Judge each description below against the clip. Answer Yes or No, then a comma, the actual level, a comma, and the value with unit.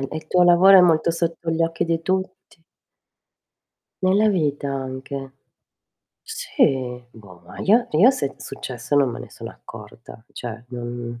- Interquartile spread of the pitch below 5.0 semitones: No, wide, 6.0 semitones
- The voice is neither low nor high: Yes, medium, 145 Hz